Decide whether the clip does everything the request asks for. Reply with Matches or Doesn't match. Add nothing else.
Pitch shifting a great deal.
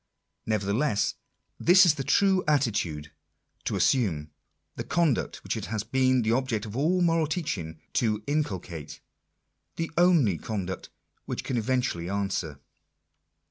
Matches